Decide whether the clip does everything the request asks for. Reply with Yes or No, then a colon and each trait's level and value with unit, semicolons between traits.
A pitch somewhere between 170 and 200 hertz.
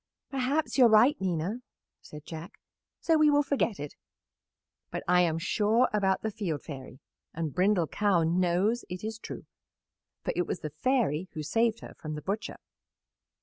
Yes: high, 190 Hz